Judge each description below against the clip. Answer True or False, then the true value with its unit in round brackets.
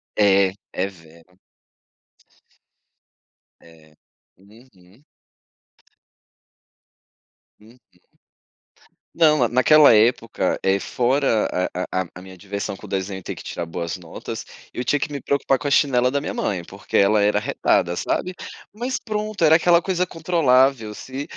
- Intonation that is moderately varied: False (7.1 semitones)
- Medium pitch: False (115 Hz)